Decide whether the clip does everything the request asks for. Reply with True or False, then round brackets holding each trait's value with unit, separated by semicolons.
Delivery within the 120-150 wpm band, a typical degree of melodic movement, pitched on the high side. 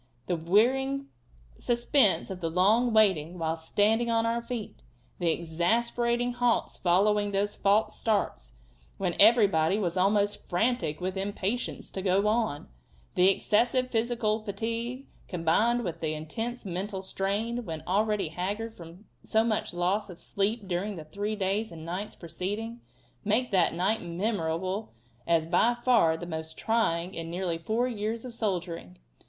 True (145 wpm; 4.5 semitones; 200 Hz)